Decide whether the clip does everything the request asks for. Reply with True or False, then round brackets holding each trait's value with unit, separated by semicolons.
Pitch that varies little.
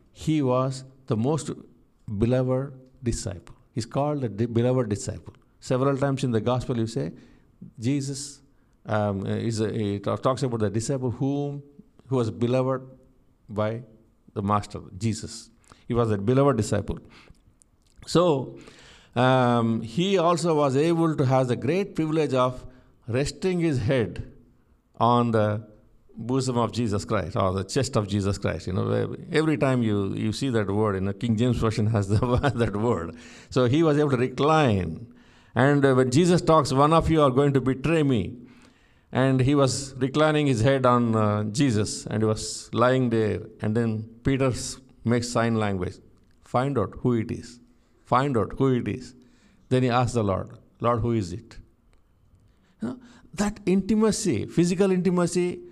False (3.9 semitones)